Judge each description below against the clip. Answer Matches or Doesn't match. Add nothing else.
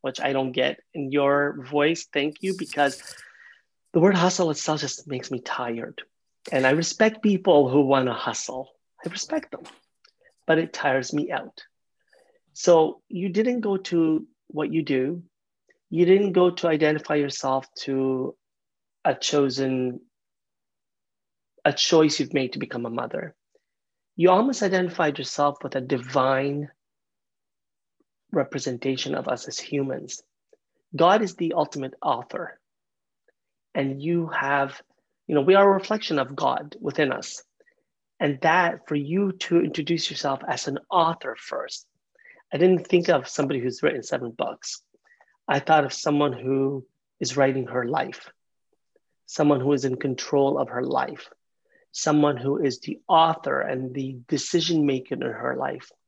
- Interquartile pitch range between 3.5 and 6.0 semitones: Matches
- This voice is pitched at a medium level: Matches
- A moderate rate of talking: Matches